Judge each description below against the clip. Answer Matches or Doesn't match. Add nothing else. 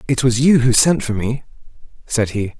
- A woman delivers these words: Doesn't match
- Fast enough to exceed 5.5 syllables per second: Doesn't match